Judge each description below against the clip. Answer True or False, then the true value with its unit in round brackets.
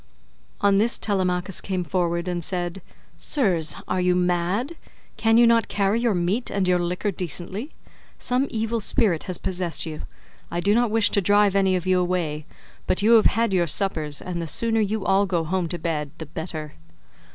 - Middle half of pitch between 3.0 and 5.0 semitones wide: True (3.3 semitones)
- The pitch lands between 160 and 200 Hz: True (185 Hz)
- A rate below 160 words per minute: False (185 wpm)